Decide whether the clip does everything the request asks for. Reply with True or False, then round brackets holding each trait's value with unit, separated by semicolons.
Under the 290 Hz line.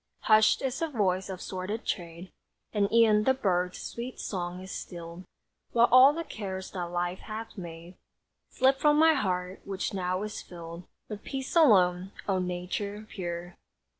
True (190 Hz)